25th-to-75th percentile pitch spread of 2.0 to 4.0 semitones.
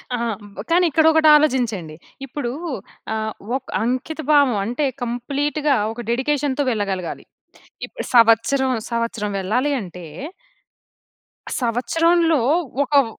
No: average, 4.4 semitones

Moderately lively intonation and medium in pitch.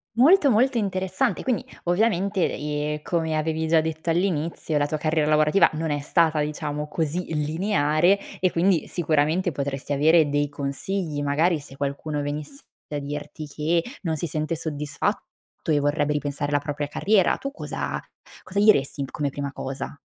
Yes: average, 3.1 semitones; medium, 155 Hz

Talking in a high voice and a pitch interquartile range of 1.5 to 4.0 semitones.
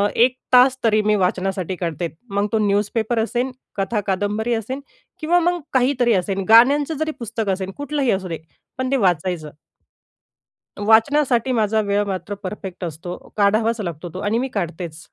No: high, 215 Hz; average, 4.6 semitones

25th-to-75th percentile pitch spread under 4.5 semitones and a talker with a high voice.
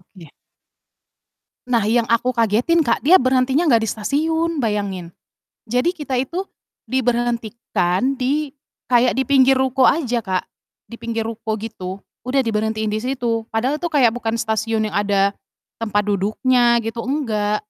Yes: average, 3.3 semitones; high, 235 Hz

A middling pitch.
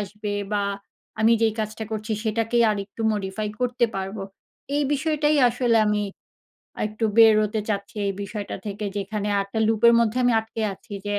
No: high, 215 Hz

